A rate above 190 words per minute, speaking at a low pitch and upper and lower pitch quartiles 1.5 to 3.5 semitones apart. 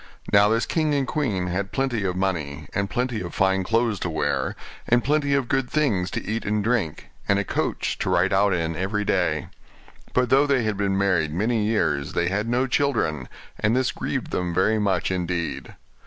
No: average, 200 wpm; low, 100 Hz; average, 5.1 semitones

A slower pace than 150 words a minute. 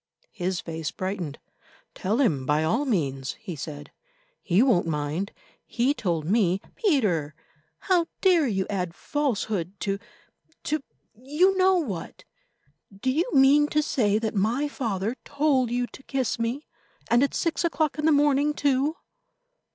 Yes: average, 140 wpm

